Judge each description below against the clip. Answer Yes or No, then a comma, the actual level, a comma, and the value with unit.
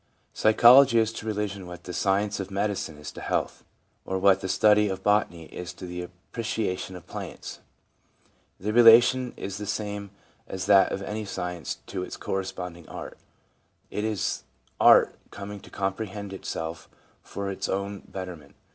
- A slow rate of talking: No, average, 155 wpm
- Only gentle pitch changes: Yes, narrow, 2.3 semitones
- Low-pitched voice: Yes, low, 100 Hz